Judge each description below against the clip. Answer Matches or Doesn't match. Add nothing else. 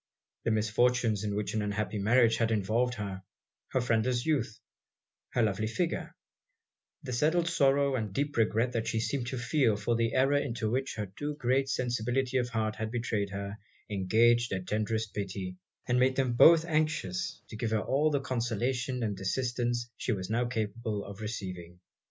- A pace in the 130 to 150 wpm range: Doesn't match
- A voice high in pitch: Doesn't match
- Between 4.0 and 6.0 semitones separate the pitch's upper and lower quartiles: Doesn't match